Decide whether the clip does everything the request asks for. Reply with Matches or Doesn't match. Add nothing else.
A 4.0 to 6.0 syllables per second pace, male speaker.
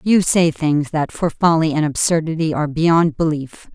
Doesn't match